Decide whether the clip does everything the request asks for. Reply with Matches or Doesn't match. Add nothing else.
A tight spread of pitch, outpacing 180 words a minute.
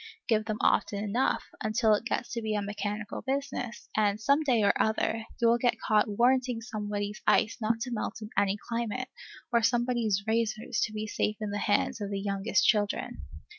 Matches